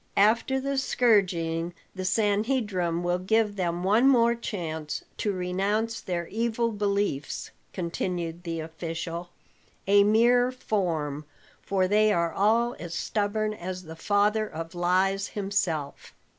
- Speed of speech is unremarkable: No, slow, 125 wpm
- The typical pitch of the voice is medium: No, high, 195 Hz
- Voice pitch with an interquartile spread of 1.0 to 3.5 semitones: No, average, 4.0 semitones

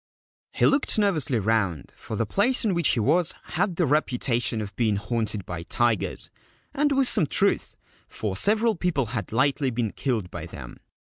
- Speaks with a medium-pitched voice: No, low, 125 Hz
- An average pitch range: No, wide, 8.6 semitones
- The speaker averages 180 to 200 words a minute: No, average, 170 wpm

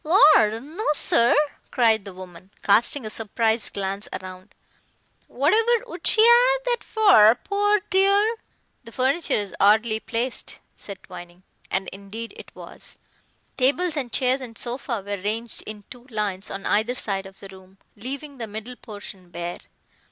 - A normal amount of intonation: No, wide, 6.4 semitones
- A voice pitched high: Yes, high, 230 Hz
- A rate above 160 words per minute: No, average, 150 wpm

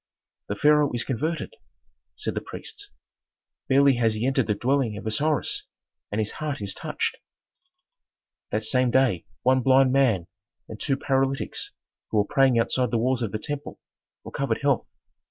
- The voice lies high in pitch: No, low, 130 Hz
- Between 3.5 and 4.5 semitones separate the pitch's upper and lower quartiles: Yes, average, 3.9 semitones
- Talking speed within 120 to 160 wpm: Yes, average, 155 wpm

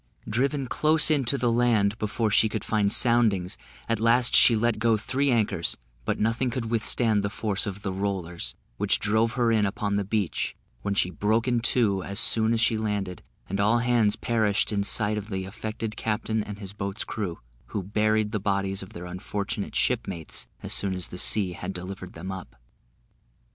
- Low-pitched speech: Yes, low, 105 Hz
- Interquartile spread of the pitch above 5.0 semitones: No, narrow, 2.6 semitones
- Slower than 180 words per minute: No, average, 190 wpm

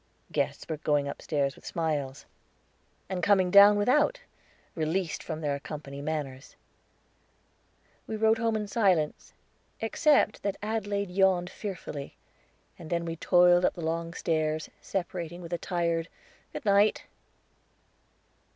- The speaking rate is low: Yes, slow, 125 wpm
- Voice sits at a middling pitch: Yes, medium, 175 Hz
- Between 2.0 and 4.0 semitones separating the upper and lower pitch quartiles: No, average, 4.4 semitones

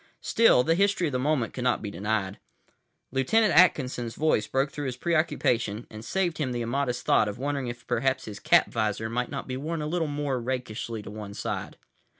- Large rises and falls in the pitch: No, average, 4.7 semitones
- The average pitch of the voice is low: Yes, low, 130 Hz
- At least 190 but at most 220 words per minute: Yes, average, 200 wpm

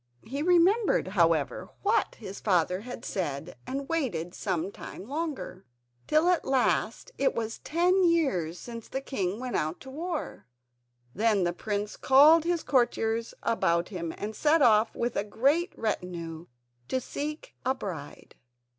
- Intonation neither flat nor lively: No, wide, 8.6 semitones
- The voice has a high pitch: Yes, high, 230 Hz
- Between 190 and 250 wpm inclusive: No, average, 145 wpm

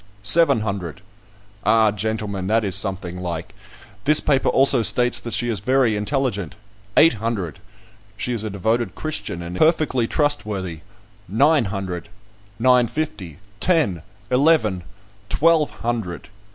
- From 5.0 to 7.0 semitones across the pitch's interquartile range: Yes, wide, 5.5 semitones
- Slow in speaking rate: Yes, slow, 125 wpm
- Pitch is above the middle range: No, low, 110 Hz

